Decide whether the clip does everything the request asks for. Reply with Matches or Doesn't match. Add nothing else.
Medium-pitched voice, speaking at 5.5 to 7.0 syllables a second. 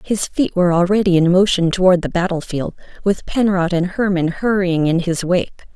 Doesn't match